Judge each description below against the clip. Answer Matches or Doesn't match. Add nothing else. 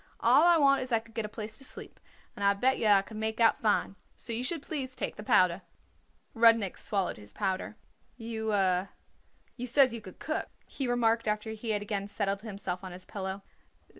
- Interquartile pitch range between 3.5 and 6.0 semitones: Doesn't match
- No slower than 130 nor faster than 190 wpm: Doesn't match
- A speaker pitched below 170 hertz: Doesn't match